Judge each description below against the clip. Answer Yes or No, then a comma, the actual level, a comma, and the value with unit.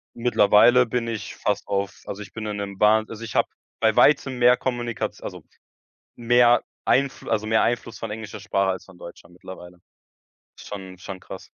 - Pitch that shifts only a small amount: No, average, 3.2 semitones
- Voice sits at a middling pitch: No, low, 110 Hz